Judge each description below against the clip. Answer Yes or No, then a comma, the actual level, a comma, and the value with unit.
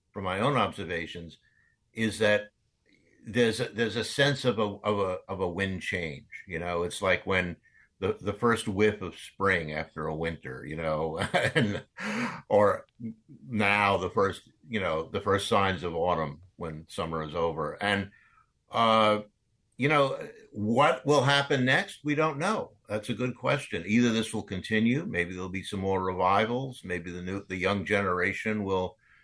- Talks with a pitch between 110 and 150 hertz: No, low, 100 Hz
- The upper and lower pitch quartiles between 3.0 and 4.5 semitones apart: Yes, average, 4.2 semitones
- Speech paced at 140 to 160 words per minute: No, average, 170 wpm